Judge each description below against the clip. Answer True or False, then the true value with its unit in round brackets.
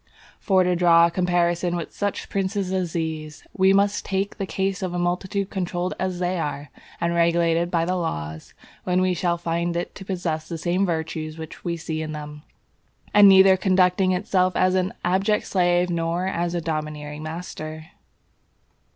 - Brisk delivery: False (175 wpm)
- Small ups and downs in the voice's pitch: True (2.1 semitones)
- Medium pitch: True (175 Hz)